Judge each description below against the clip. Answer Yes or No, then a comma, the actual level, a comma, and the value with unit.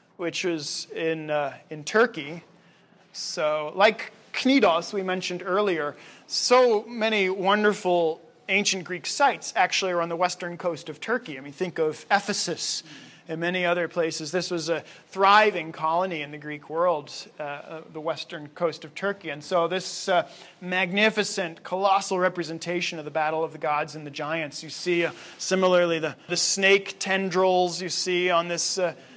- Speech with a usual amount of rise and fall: Yes, average, 3.0 semitones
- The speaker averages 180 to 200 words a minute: No, average, 165 wpm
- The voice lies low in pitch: No, medium, 175 Hz